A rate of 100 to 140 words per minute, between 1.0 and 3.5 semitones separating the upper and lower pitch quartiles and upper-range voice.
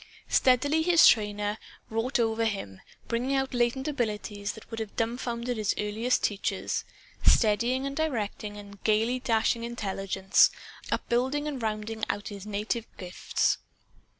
Yes: slow, 135 wpm; average, 3.2 semitones; high, 225 Hz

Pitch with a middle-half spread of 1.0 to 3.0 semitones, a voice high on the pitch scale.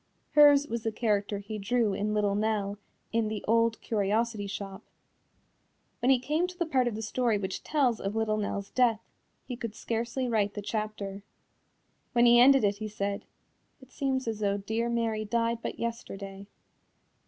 Yes: average, 2.7 semitones; high, 220 Hz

